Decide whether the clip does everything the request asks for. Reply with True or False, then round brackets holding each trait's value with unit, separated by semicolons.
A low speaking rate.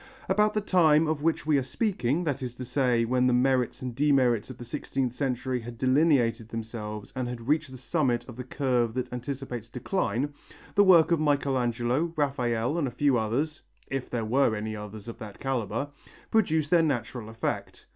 False (185 wpm)